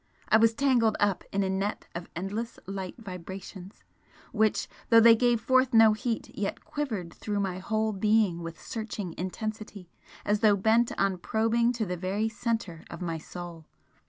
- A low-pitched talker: No, high, 210 Hz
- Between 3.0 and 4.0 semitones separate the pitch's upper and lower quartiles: Yes, average, 3.3 semitones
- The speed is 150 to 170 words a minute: Yes, average, 165 wpm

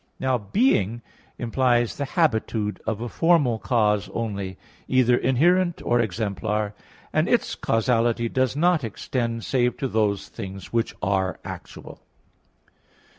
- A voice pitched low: Yes, low, 115 Hz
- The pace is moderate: No, slow, 125 wpm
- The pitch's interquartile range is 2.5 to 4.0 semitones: Yes, average, 3.6 semitones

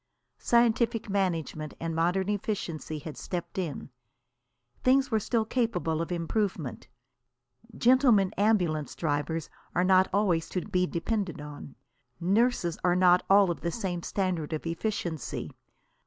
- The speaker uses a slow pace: Yes, slow, 125 wpm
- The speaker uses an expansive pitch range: No, average, 4.2 semitones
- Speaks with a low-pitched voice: No, medium, 180 Hz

